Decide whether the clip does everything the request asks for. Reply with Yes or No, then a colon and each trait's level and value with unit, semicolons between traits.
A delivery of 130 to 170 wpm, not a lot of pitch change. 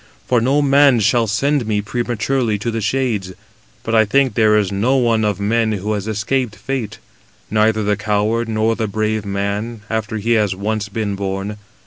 No: average, 180 wpm; narrow, 2.3 semitones